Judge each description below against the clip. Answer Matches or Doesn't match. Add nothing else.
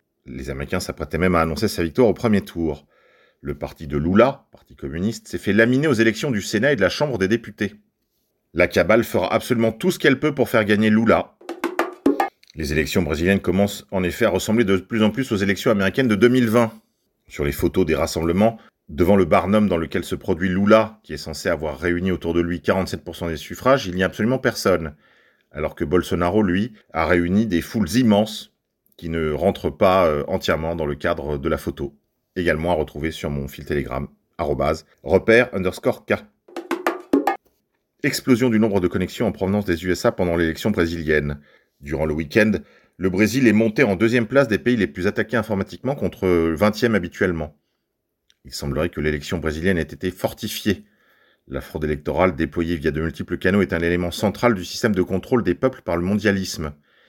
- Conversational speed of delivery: Matches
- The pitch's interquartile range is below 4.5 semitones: Doesn't match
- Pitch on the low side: Matches